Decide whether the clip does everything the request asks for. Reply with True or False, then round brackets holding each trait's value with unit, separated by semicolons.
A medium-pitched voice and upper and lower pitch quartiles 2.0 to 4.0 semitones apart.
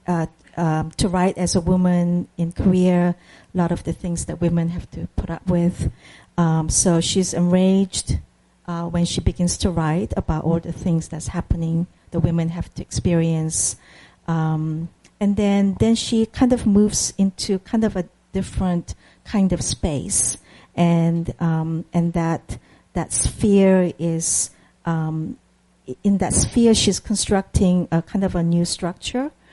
True (175 Hz; 2.5 semitones)